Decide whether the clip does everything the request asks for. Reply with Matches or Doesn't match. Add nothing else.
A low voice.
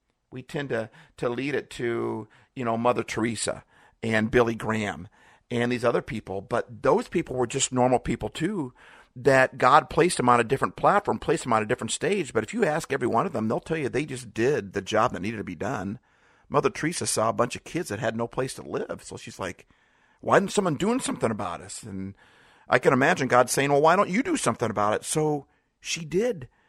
Matches